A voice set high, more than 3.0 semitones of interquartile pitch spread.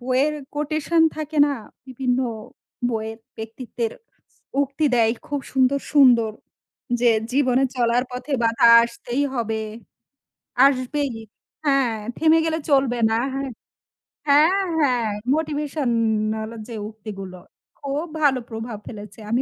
Yes: very high, 255 Hz; average, 3.8 semitones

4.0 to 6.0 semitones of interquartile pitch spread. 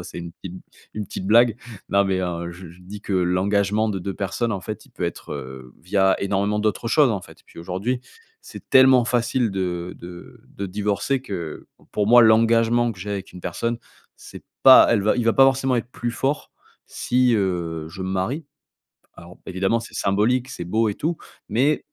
Yes: average, 4.3 semitones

